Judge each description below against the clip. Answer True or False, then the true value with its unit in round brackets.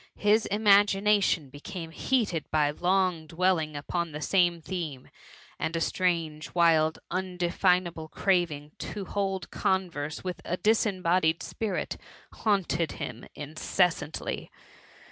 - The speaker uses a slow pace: True (125 wpm)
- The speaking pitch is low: False (175 Hz)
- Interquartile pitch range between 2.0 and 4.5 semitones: True (3.2 semitones)